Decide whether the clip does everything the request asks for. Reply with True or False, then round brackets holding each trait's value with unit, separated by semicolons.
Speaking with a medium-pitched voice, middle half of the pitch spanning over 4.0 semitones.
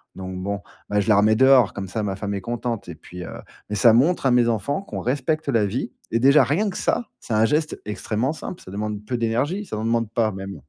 False (115 Hz; 4.6 semitones)